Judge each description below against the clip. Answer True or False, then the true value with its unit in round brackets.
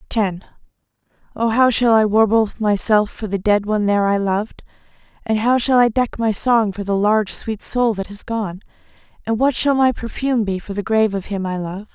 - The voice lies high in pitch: True (215 Hz)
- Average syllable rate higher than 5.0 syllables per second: True (5.4 syllables/s)